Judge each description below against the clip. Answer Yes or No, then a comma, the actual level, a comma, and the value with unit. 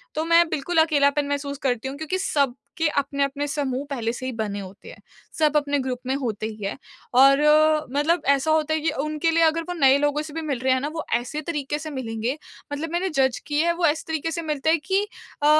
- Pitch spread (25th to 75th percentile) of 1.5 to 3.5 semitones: Yes, average, 3.0 semitones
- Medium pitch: No, very high, 290 Hz